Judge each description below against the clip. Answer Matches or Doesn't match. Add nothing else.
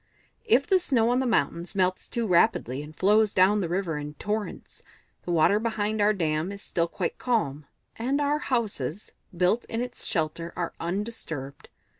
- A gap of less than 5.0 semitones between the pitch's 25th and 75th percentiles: Doesn't match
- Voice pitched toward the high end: Matches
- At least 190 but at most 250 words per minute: Doesn't match